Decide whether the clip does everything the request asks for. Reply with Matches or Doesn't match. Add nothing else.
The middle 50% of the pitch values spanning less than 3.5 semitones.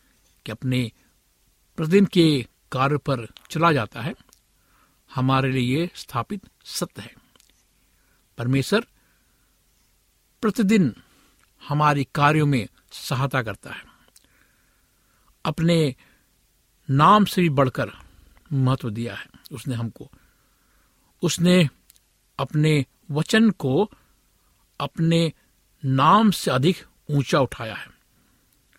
Doesn't match